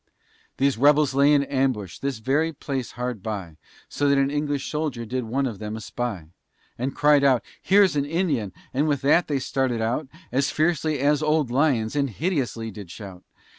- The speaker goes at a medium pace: Yes, average, 175 wpm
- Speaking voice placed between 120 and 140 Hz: Yes, low, 135 Hz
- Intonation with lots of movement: No, average, 4.0 semitones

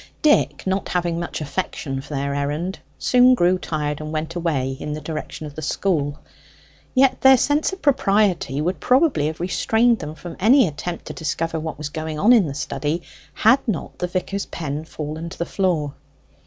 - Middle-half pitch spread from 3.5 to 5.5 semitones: Yes, average, 4.7 semitones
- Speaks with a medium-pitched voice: Yes, medium, 165 Hz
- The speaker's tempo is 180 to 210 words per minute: Yes, average, 185 wpm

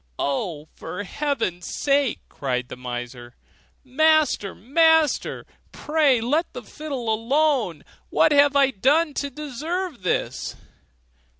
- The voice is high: Yes, very high, 270 Hz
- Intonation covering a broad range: Yes, wide, 8.7 semitones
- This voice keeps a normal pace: No, slow, 110 wpm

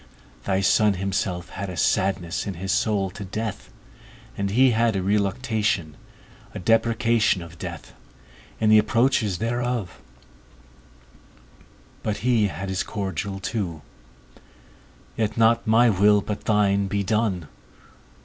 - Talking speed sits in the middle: No, slow, 125 wpm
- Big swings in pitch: No, average, 2.8 semitones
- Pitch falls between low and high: No, low, 100 Hz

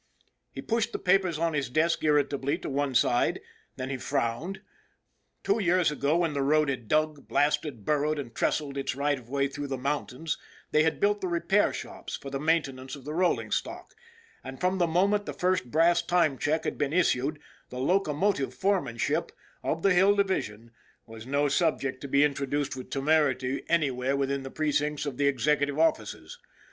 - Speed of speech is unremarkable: Yes, average, 180 wpm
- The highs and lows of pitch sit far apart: No, average, 3.7 semitones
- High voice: No, medium, 145 Hz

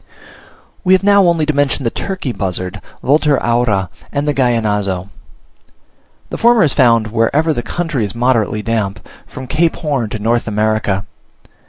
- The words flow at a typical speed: Yes, average, 155 wpm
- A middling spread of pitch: No, wide, 5.9 semitones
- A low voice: Yes, low, 120 Hz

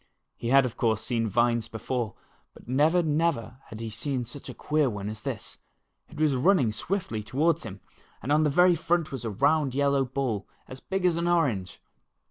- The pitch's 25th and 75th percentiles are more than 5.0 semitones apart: Yes, wide, 5.5 semitones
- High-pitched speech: No, low, 130 Hz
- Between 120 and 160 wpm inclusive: No, average, 200 wpm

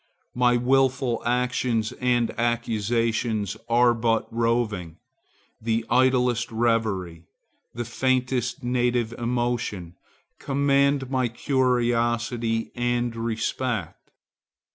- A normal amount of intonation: No, narrow, 1.6 semitones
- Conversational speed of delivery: No, slow, 75 wpm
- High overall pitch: No, low, 120 Hz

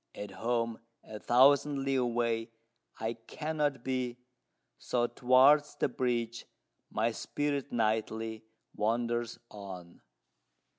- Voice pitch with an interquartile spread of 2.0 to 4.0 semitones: Yes, average, 2.7 semitones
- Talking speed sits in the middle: No, slow, 100 wpm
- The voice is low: Yes, low, 120 Hz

